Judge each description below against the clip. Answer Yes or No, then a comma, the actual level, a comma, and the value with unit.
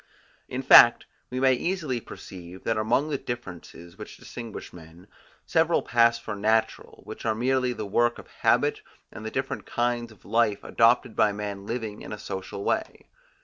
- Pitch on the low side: Yes, low, 115 Hz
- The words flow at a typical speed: Yes, average, 170 wpm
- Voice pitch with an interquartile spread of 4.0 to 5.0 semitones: No, average, 3.2 semitones